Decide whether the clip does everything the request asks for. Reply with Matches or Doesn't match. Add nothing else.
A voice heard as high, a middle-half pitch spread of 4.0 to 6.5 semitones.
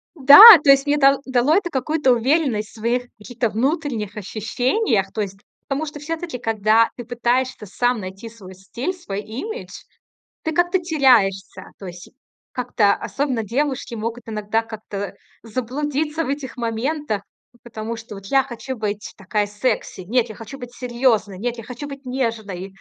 Matches